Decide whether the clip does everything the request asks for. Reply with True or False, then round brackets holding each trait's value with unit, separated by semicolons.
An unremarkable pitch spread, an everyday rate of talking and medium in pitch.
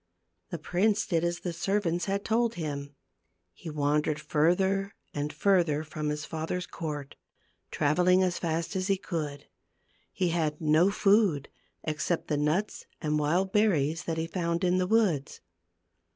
True (3.8 semitones; 150 wpm; 170 Hz)